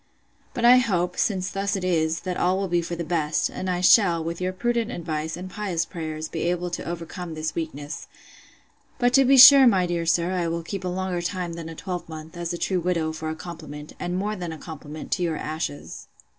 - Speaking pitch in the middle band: Yes, medium, 175 Hz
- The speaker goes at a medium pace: No, fast, 220 wpm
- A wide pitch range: No, narrow, 2.4 semitones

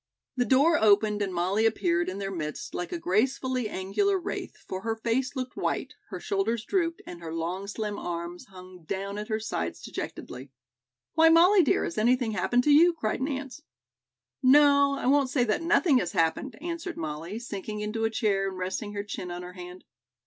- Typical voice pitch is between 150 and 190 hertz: No, high, 215 Hz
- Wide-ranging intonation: Yes, wide, 6.6 semitones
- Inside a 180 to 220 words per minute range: Yes, average, 190 wpm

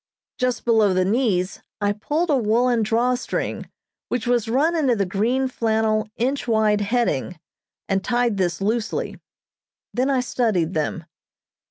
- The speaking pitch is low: No, high, 225 Hz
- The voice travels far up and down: No, average, 3.6 semitones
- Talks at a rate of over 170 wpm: No, average, 140 wpm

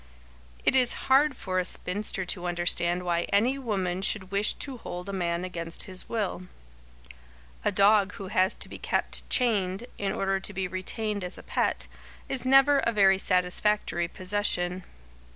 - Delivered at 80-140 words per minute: No, average, 165 wpm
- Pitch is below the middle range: No, high, 195 Hz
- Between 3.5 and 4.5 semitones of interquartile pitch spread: No, average, 2.8 semitones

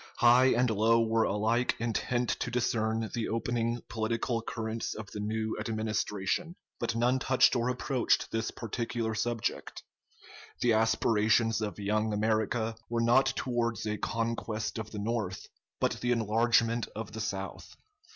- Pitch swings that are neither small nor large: No, narrow, 1.4 semitones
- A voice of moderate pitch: No, low, 115 Hz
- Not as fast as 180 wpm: Yes, average, 140 wpm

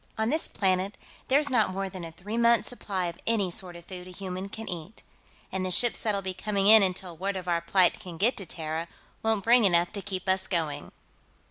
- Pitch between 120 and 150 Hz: No, high, 190 Hz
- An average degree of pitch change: Yes, average, 3.1 semitones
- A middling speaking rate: No, fast, 225 wpm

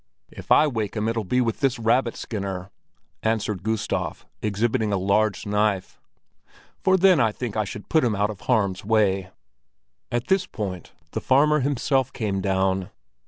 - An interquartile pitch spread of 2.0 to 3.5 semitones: No, average, 4.0 semitones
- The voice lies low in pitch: Yes, low, 110 Hz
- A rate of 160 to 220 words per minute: Yes, average, 165 wpm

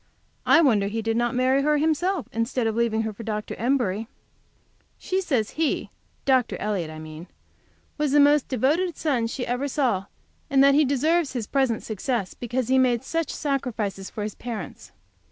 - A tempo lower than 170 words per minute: No, average, 180 wpm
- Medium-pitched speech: No, very high, 250 Hz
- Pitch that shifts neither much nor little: Yes, average, 4.3 semitones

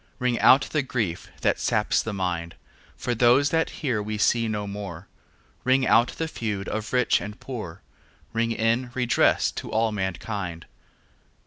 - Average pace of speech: Yes, average, 155 wpm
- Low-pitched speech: Yes, low, 110 Hz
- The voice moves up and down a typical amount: Yes, average, 3.8 semitones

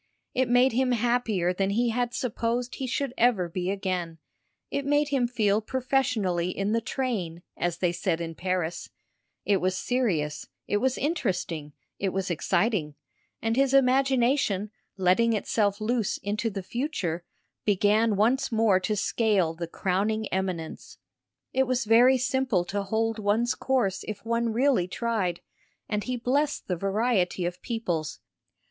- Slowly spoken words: No, average, 150 wpm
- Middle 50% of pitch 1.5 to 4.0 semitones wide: No, average, 5.1 semitones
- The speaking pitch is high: Yes, high, 215 Hz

